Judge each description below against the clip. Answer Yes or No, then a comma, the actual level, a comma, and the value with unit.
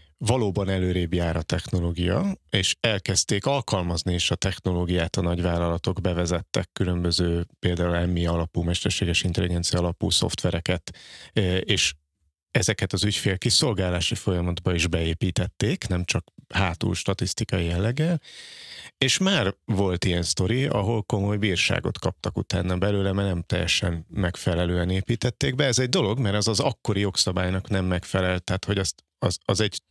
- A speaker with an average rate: Yes, average, 135 wpm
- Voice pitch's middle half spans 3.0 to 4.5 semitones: Yes, average, 3.3 semitones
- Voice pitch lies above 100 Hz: No, very low, 95 Hz